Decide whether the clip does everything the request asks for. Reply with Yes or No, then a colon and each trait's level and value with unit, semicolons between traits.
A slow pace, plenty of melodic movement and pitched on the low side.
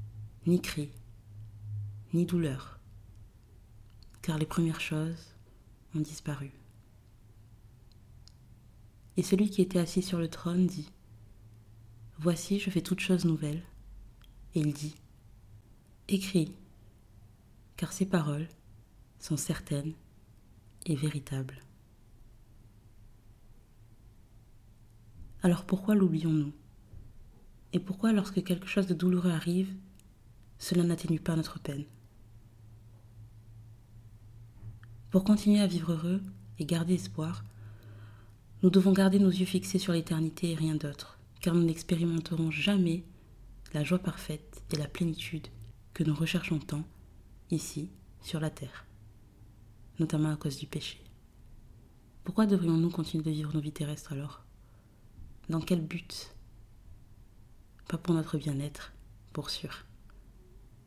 Yes: slow, 110 wpm; wide, 7.5 semitones; low, 125 Hz